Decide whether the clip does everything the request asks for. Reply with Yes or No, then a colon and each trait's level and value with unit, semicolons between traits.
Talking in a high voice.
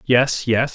No: low, 120 Hz